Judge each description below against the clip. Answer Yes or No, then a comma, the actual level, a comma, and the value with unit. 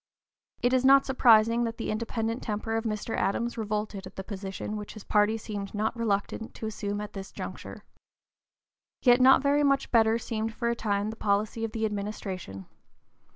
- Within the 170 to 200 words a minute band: Yes, average, 180 wpm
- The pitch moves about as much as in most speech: No, narrow, 2.0 semitones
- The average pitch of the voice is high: Yes, high, 220 Hz